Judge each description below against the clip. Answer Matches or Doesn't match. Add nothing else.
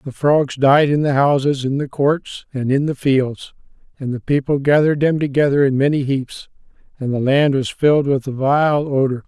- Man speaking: Matches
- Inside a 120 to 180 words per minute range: Doesn't match